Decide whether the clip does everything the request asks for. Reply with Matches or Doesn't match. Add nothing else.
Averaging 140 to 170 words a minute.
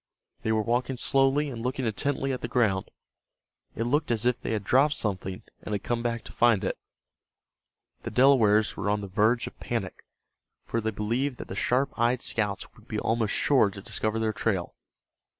Doesn't match